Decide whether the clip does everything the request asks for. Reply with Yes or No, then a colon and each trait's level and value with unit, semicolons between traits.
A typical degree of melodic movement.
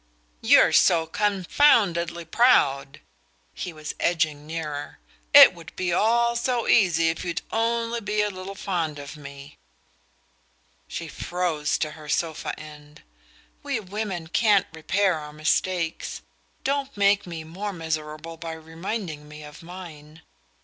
Yes: average, 4.7 semitones